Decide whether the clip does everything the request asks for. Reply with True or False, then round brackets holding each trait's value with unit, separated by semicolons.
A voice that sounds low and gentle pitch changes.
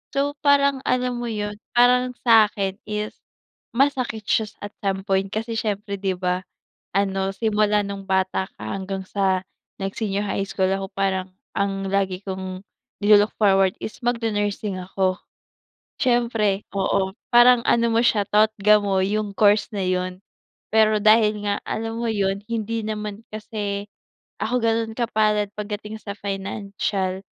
False (205 Hz; 2.3 semitones)